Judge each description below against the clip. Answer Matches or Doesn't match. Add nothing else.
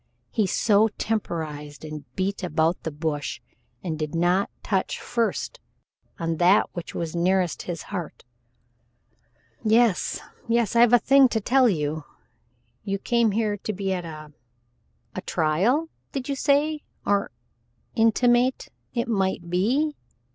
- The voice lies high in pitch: Matches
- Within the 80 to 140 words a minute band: Matches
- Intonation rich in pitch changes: Matches